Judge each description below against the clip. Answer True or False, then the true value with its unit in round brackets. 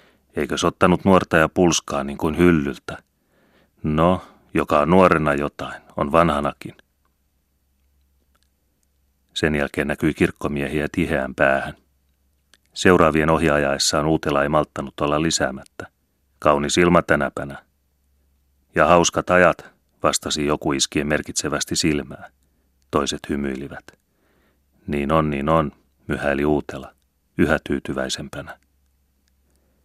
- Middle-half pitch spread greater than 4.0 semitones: False (2.4 semitones)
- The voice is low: True (70 Hz)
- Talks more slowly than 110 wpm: True (100 wpm)